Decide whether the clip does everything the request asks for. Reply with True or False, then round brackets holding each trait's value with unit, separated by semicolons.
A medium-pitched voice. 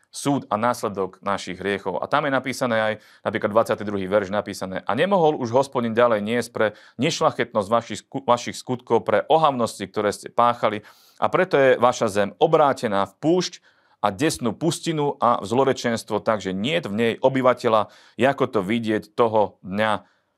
False (115 Hz)